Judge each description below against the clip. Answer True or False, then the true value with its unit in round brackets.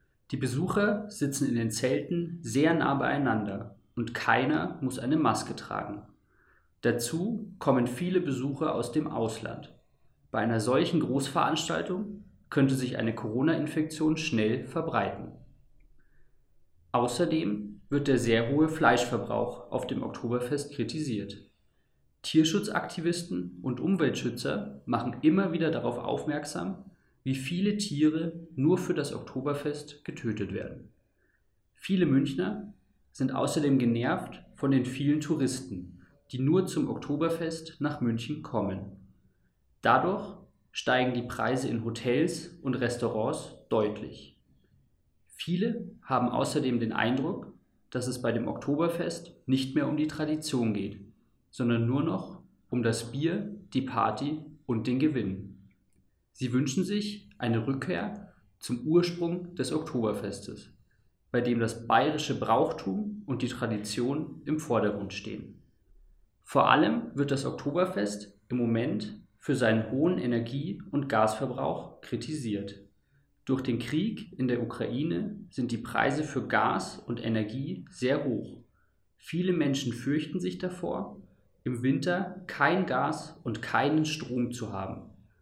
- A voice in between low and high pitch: False (130 Hz)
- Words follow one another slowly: True (120 wpm)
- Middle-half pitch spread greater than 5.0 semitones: True (5.4 semitones)